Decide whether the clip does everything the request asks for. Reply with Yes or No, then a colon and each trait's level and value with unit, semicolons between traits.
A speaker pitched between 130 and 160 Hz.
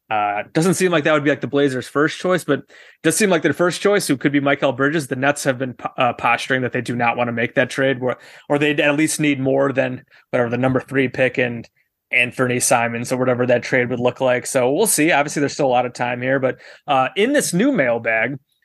Yes: low, 135 Hz